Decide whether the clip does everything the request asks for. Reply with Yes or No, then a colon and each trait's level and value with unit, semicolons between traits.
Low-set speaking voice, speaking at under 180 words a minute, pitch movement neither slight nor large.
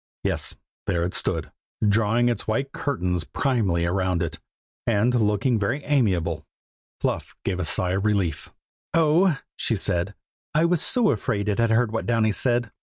Yes: low, 110 Hz; average, 160 wpm; average, 5.0 semitones